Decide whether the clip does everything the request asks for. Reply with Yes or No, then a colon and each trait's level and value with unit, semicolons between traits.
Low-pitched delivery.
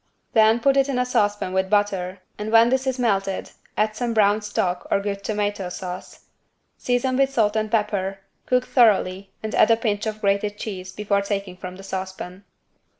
No: high, 205 Hz